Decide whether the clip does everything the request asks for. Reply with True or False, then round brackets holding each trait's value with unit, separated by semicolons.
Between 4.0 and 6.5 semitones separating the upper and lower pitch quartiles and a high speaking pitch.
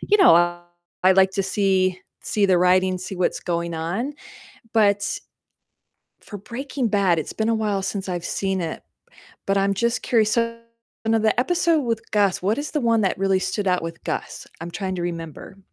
False (3.5 semitones; 195 Hz)